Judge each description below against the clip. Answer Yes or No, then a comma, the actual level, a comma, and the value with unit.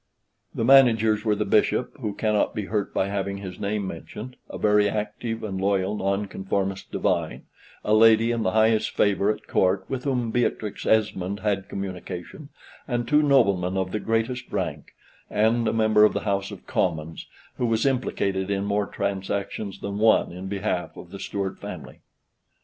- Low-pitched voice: Yes, low, 105 Hz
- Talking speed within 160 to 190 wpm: Yes, average, 170 wpm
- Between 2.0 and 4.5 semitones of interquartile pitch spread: Yes, narrow, 2.4 semitones